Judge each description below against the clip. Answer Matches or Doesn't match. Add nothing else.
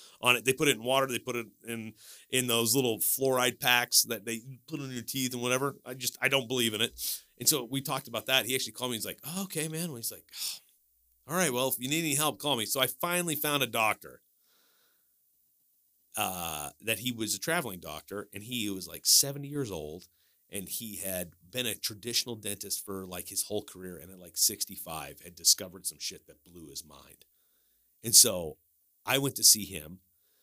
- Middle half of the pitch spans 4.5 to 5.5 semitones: Matches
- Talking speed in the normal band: Doesn't match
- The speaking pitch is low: Matches